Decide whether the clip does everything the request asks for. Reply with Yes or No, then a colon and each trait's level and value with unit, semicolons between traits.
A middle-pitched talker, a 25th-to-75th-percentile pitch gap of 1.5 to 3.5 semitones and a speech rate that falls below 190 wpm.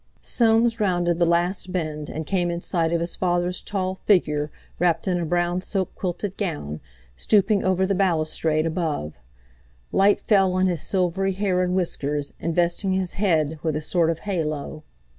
Yes: medium, 175 Hz; average, 2.8 semitones; average, 165 wpm